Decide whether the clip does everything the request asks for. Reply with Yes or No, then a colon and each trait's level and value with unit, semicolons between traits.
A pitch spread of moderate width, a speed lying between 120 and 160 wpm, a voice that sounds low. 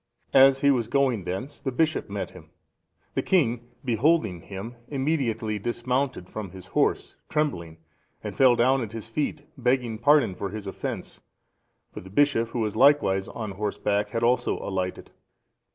Yes: average, 4.9 semitones; average, 155 wpm; low, 115 Hz